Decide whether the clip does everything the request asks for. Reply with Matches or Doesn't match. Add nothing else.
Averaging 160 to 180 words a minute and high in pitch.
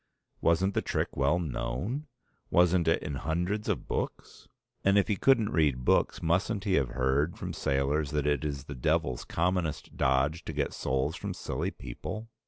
Doesn't match